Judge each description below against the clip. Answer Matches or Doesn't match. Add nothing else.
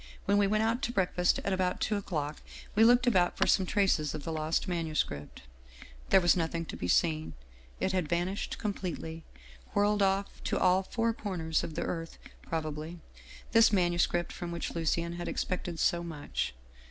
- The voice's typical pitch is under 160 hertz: Doesn't match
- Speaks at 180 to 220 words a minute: Matches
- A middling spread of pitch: Matches